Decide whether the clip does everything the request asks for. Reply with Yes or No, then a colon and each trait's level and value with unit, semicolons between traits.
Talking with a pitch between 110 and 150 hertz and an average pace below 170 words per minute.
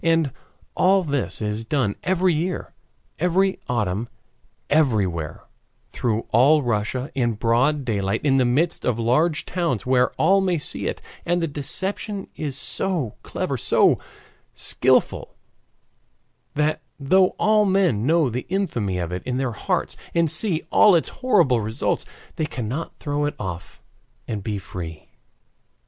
Yes: medium, 140 Hz; average, 140 wpm